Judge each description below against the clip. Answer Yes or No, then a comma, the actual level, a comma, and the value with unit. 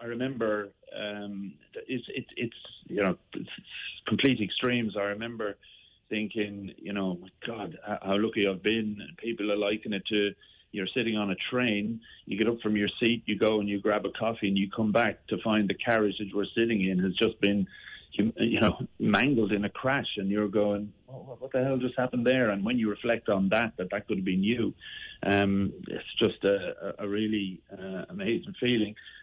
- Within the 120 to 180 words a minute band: No, average, 200 wpm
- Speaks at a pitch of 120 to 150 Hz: No, low, 105 Hz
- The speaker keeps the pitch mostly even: Yes, narrow, 2.1 semitones